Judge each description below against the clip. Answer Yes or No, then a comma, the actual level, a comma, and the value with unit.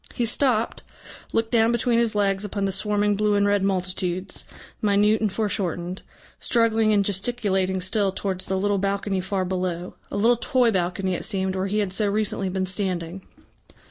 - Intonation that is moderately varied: No, narrow, 2.2 semitones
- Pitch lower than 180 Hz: No, high, 200 Hz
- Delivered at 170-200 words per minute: Yes, average, 175 wpm